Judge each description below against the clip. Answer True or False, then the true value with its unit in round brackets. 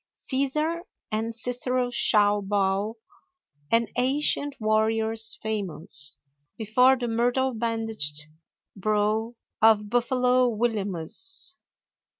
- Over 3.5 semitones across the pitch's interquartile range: False (3.0 semitones)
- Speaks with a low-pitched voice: False (225 Hz)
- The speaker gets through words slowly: True (85 wpm)